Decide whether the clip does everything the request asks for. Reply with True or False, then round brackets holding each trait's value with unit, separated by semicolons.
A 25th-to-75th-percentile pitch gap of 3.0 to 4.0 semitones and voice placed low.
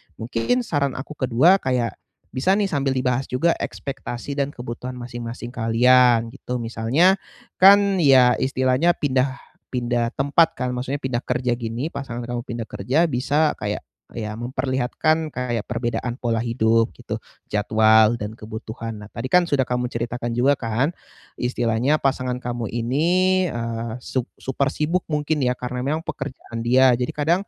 True (3.3 semitones; 125 Hz)